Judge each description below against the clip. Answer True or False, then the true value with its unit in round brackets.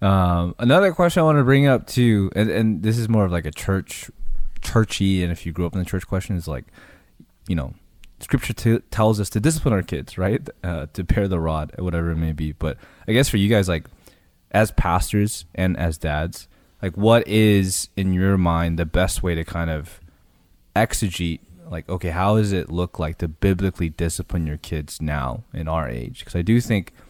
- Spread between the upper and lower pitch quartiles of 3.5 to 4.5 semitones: True (4.1 semitones)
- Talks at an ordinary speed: False (210 wpm)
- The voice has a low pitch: True (90 Hz)